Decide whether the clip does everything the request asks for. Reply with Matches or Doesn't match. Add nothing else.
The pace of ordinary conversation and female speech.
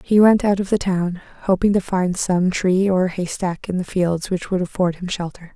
Doesn't match